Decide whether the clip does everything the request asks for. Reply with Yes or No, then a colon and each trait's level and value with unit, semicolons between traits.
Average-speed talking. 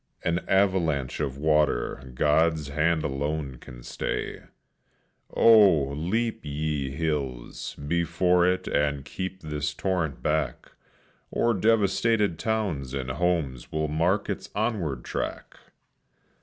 No: slow, 110 wpm